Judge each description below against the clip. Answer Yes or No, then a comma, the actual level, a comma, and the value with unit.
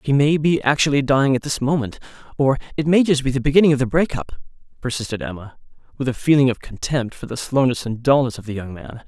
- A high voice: No, low, 135 Hz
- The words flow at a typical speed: No, fast, 225 wpm